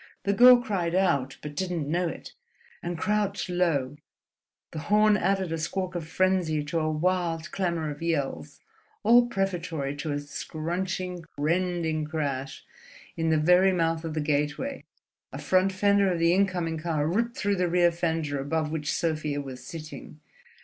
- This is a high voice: No, medium, 170 Hz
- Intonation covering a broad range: No, average, 3.3 semitones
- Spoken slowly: No, average, 165 wpm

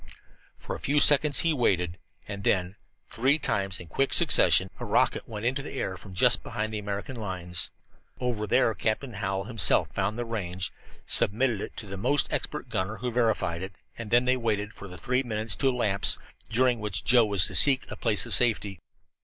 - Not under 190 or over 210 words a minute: Yes, average, 195 wpm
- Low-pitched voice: Yes, low, 110 Hz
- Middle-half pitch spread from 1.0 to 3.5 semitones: No, average, 4.2 semitones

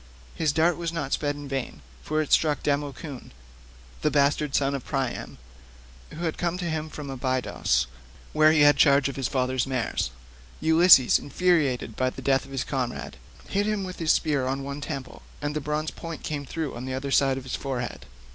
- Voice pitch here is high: No, medium, 140 Hz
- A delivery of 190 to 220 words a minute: Yes, average, 195 wpm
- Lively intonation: No, average, 2.7 semitones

